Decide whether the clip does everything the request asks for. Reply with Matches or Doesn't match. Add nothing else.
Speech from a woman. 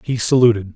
Doesn't match